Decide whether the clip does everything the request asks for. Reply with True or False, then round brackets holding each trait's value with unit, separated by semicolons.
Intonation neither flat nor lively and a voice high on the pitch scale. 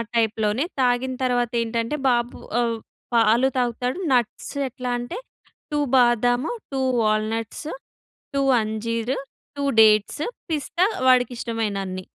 False (2.3 semitones; 240 Hz)